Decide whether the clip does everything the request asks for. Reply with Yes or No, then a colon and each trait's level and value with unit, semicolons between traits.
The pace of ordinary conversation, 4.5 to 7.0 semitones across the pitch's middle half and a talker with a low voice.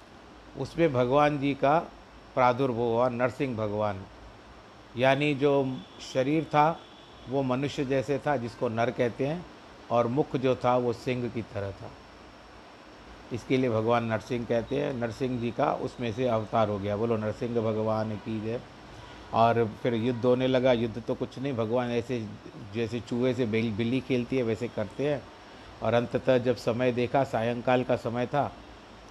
No: average, 160 wpm; narrow, 2.4 semitones; low, 125 Hz